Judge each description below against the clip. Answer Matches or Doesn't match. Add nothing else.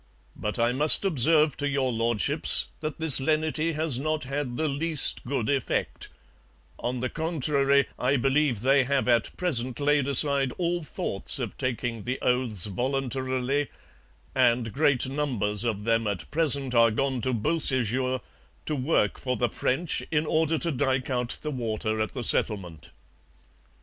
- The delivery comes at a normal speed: Matches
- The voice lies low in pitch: Matches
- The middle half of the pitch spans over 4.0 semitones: Doesn't match